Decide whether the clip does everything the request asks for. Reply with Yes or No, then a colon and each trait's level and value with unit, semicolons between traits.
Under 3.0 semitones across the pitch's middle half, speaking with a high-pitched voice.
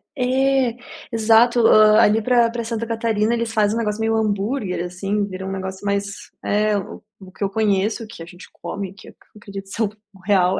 Yes: narrow, 2.4 semitones; high, 210 Hz